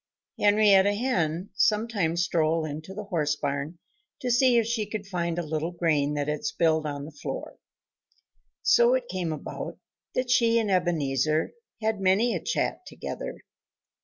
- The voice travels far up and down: Yes, wide, 5.7 semitones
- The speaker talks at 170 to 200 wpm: No, average, 155 wpm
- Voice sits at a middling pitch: Yes, medium, 175 Hz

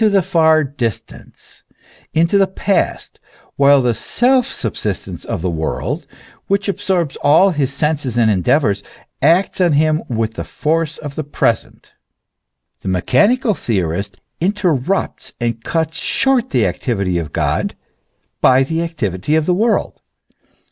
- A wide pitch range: Yes, wide, 7.8 semitones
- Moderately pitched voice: Yes, medium, 150 Hz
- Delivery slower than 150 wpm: Yes, slow, 135 wpm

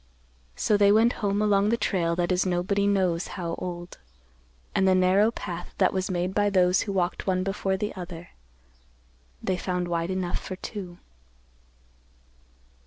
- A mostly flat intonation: Yes, narrow, 2.2 semitones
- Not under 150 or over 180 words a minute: Yes, average, 160 wpm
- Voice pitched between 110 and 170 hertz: No, medium, 185 Hz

